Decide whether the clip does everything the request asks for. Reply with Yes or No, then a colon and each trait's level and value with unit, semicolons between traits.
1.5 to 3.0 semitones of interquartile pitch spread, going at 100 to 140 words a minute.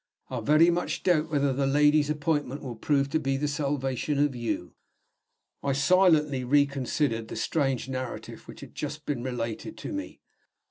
No: narrow, 2.5 semitones; average, 165 wpm